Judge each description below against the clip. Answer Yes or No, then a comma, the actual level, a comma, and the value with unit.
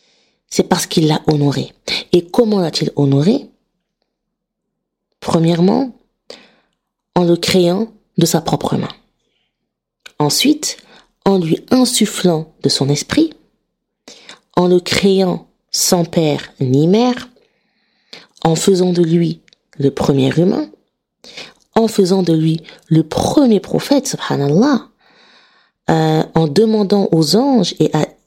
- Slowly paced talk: Yes, slow, 115 wpm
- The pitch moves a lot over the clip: Yes, wide, 5.7 semitones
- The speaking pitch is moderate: Yes, medium, 180 Hz